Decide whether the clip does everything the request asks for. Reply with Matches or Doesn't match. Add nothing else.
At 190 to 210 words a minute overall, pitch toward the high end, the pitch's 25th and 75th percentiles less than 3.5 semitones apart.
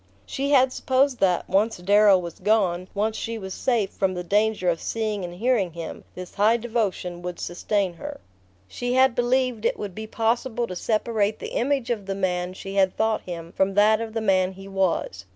Doesn't match